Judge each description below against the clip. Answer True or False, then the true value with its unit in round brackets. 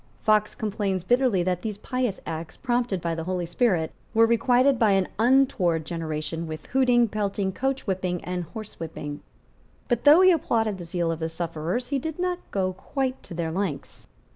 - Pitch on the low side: False (195 Hz)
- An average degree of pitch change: False (6.2 semitones)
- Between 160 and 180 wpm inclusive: True (170 wpm)